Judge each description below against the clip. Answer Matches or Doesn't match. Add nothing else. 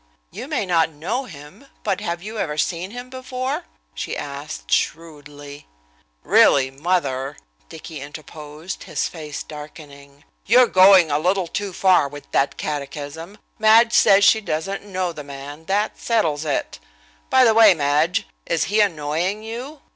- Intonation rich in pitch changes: Matches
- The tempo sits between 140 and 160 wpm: Matches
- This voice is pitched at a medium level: Matches